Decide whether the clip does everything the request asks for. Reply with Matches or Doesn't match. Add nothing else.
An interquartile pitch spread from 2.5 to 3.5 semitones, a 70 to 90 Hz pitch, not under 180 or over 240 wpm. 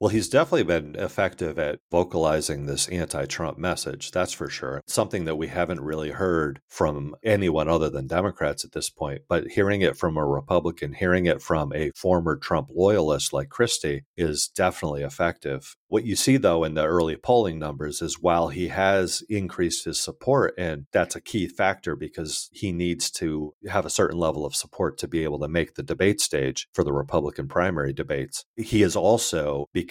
Matches